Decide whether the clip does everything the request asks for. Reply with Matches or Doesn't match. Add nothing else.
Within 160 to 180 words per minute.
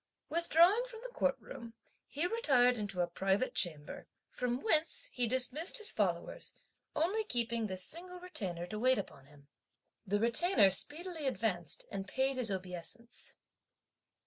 Doesn't match